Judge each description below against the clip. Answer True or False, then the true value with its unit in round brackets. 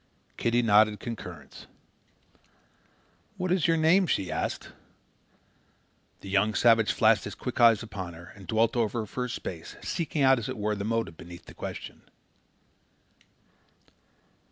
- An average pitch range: True (3.4 semitones)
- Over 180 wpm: False (145 wpm)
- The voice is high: False (110 Hz)